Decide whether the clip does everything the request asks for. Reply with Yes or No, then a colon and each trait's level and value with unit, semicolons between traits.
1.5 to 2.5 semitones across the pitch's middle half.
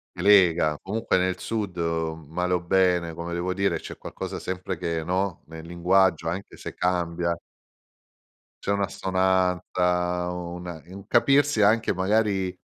Yes: narrow, 2.0 semitones